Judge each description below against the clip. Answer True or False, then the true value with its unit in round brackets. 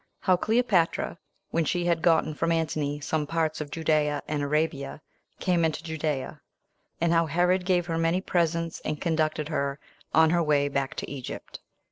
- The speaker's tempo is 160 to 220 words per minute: True (165 wpm)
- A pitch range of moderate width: False (2.2 semitones)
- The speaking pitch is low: False (160 Hz)